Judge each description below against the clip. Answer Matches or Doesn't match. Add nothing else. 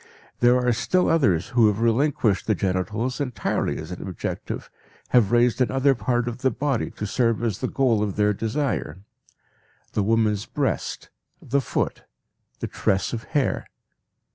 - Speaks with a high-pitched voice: Doesn't match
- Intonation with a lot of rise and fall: Doesn't match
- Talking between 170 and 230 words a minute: Doesn't match